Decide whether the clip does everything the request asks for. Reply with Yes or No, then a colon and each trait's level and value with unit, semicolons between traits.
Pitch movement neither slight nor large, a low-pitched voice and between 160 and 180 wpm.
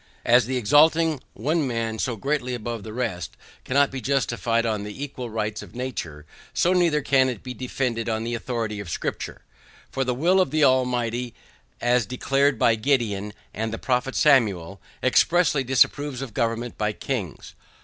Yes: average, 3.4 semitones; low, 125 Hz; average, 170 wpm